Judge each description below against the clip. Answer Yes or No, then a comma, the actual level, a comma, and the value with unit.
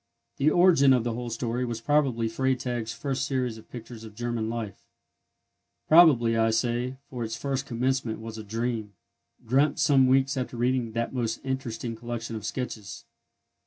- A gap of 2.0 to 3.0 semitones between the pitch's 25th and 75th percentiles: Yes, narrow, 2.6 semitones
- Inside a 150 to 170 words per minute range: Yes, average, 160 wpm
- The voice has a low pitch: Yes, low, 120 Hz